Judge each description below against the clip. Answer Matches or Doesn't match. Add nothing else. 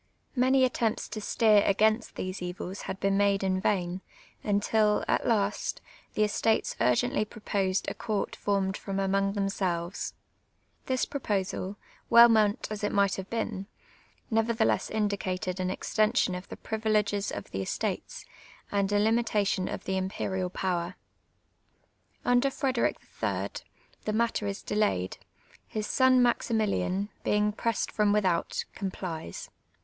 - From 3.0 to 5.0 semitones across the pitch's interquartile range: Doesn't match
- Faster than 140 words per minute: Doesn't match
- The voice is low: Doesn't match